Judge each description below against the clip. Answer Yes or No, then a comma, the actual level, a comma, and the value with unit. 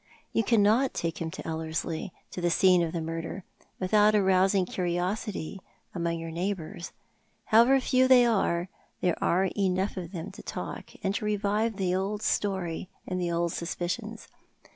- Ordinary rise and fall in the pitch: Yes, average, 3.5 semitones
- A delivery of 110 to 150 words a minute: No, average, 165 wpm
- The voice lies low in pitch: No, medium, 185 Hz